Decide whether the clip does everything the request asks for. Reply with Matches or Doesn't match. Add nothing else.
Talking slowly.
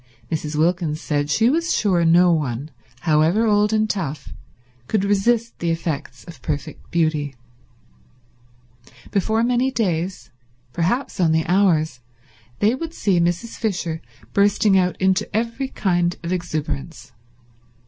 Matches